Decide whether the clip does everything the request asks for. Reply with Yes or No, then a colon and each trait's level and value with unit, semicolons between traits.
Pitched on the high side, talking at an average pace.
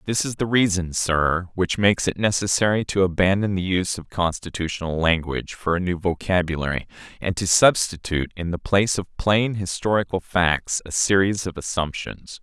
No: very low, 90 Hz; average, 165 wpm